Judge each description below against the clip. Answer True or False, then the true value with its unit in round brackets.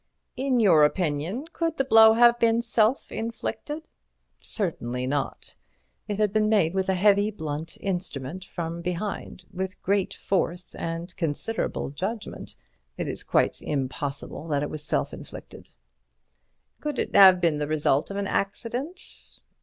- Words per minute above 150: False (145 wpm)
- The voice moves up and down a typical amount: False (5.9 semitones)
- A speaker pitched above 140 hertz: True (190 Hz)